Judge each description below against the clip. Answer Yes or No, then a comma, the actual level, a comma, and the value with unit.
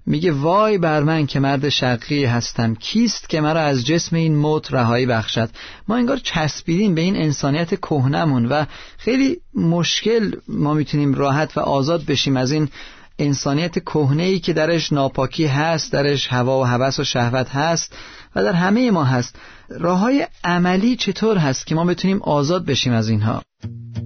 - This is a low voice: No, medium, 150 Hz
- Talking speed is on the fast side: Yes, fast, 160 wpm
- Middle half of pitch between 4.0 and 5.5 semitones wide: Yes, average, 4.7 semitones